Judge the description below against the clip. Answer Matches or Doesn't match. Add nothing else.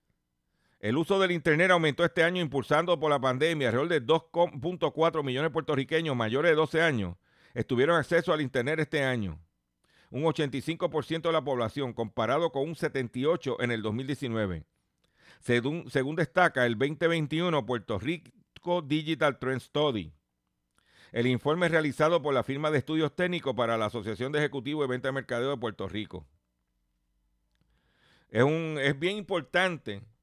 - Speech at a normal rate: Matches